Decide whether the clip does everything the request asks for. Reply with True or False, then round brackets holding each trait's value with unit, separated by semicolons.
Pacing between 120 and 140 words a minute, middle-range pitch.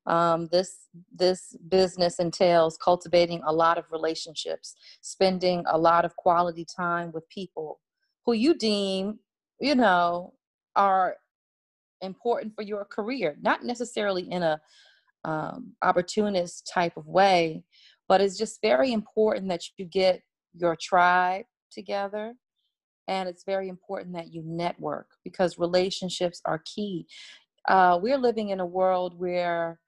True (135 wpm; 180 Hz)